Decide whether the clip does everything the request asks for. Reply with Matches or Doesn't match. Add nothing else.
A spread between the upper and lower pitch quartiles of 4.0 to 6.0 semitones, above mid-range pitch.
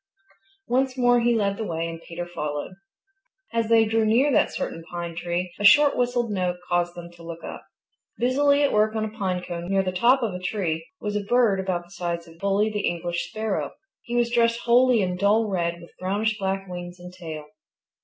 Matches